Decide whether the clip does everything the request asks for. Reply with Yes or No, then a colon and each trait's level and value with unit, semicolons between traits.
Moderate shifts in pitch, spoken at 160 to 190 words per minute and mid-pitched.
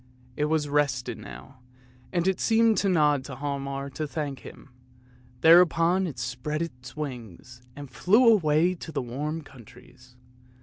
No: average, 4.3 semitones; average, 145 wpm; medium, 145 Hz